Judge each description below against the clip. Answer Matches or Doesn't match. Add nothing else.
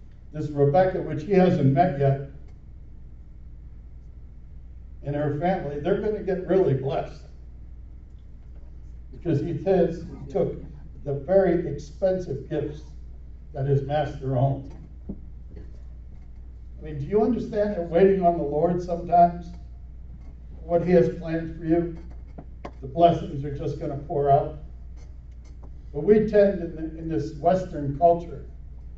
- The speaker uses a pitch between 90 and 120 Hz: Doesn't match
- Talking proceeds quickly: Doesn't match